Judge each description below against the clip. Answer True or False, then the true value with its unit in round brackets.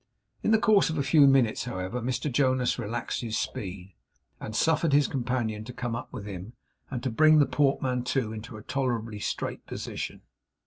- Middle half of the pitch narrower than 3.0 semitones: False (3.8 semitones)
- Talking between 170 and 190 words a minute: True (180 wpm)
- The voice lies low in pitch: True (125 Hz)